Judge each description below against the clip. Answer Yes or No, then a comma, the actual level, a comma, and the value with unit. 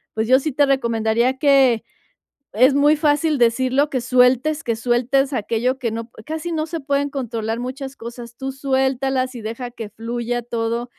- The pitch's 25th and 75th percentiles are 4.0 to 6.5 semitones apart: No, average, 2.9 semitones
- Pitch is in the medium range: No, very high, 255 Hz